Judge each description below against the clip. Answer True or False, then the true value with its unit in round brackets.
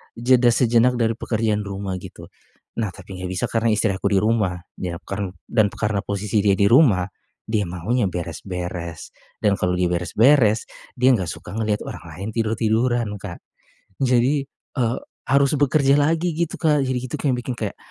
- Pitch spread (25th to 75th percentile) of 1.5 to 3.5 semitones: False (4.4 semitones)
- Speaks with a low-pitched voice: True (110 Hz)